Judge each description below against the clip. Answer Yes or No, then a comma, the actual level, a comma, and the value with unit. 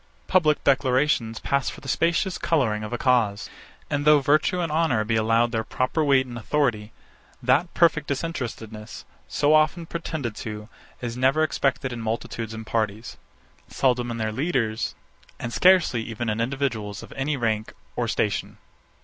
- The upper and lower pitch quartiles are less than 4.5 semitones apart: No, average, 5.1 semitones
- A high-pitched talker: No, low, 125 Hz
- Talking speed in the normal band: Yes, average, 160 wpm